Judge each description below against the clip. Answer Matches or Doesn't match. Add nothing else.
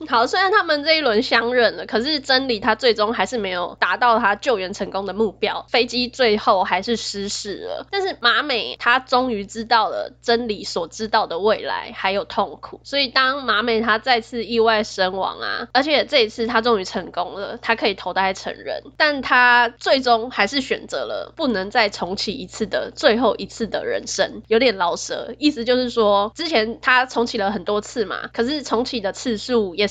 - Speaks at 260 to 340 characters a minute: Matches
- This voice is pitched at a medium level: Doesn't match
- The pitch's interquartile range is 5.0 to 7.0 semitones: Doesn't match